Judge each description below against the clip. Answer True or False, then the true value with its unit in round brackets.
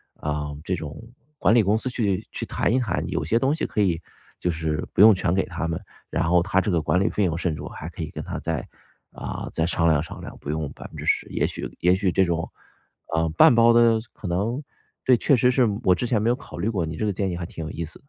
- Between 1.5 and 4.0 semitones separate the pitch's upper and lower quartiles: False (5.3 semitones)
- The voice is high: False (90 Hz)